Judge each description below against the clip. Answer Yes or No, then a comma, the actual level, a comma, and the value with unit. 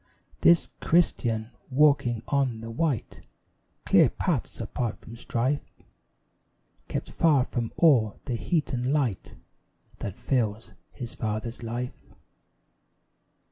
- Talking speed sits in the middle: No, slow, 105 wpm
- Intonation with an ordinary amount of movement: Yes, average, 3.7 semitones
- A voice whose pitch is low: Yes, low, 120 Hz